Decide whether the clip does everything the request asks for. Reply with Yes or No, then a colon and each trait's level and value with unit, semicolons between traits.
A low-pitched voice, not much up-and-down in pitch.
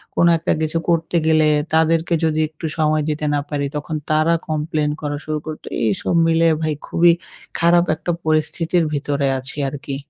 No: medium, 155 Hz; narrow, 1.7 semitones